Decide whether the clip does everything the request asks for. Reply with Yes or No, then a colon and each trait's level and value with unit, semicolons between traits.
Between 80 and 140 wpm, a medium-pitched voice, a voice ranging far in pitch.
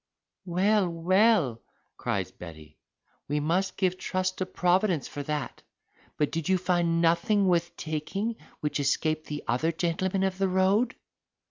No: slow, 135 wpm; medium, 175 Hz; average, 3.5 semitones